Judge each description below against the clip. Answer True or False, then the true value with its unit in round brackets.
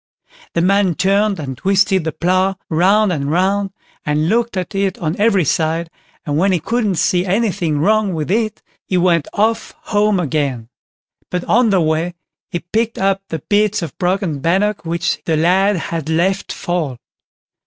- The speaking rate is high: False (165 wpm)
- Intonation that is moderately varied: True (3.6 semitones)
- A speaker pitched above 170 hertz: True (185 Hz)